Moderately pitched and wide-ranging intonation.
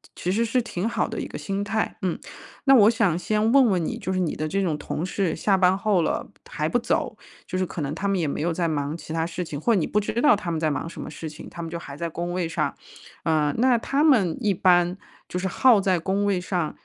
No: medium, 180 Hz; average, 4.0 semitones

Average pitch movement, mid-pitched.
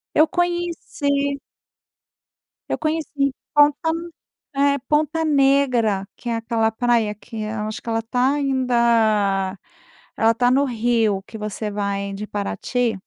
No: average, 4.6 semitones; high, 235 Hz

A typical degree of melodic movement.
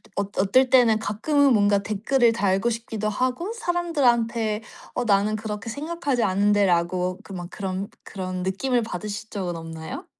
Yes: average, 4.0 semitones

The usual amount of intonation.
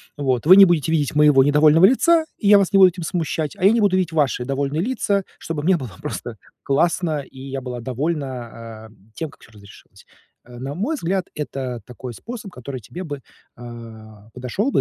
No: wide, 6.4 semitones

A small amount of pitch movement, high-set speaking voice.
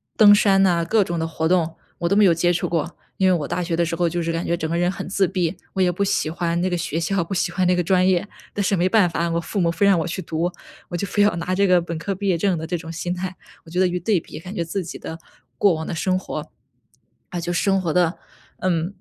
No: narrow, 2.2 semitones; medium, 175 Hz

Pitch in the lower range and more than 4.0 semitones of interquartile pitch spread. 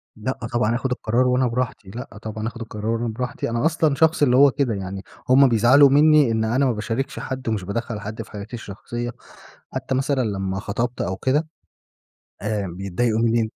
No: low, 120 Hz; average, 3.3 semitones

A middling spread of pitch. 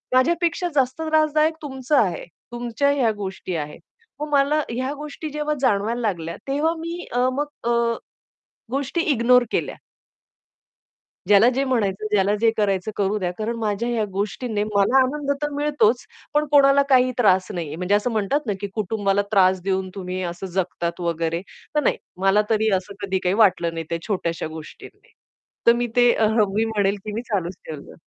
No: wide, 5.9 semitones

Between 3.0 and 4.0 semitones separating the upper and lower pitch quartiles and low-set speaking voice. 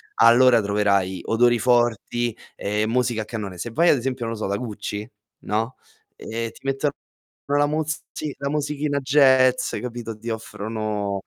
Yes: average, 3.6 semitones; low, 115 Hz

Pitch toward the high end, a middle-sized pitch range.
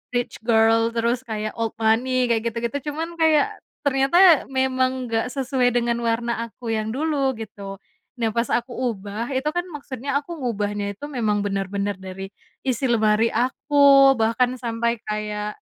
Yes: high, 235 Hz; average, 3.3 semitones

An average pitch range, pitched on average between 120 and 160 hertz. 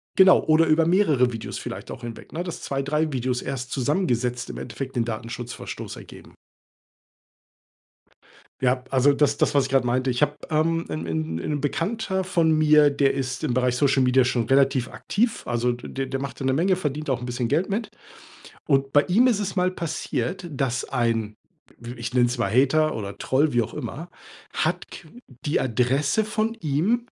Yes: average, 4.4 semitones; low, 135 Hz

